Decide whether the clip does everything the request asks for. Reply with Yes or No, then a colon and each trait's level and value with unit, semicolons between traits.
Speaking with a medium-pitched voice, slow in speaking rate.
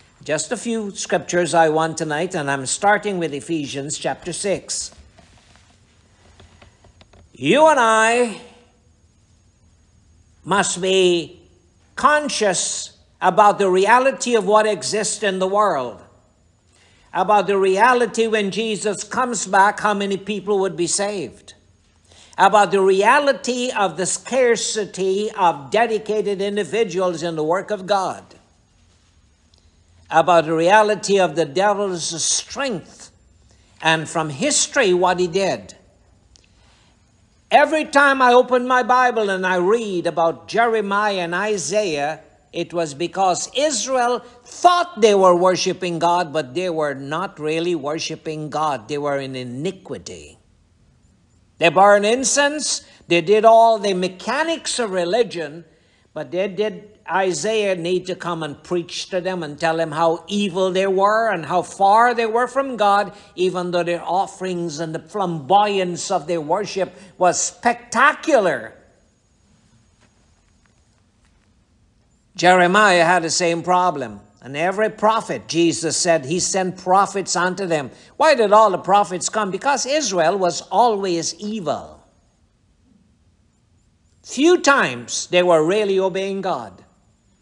Yes: medium, 180 Hz; slow, 125 wpm